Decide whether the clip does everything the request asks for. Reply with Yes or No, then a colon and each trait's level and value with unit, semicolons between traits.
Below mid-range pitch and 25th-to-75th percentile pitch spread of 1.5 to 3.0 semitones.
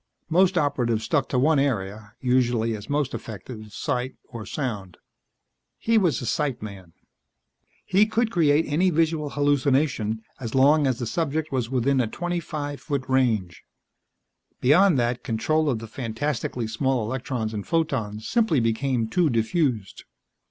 No: low, 130 Hz; average, 5.1 semitones